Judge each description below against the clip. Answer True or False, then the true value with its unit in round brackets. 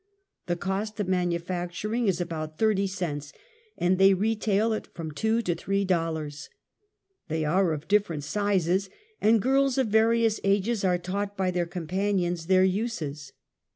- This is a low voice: False (190 Hz)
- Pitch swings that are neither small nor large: True (3.5 semitones)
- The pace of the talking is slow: False (155 wpm)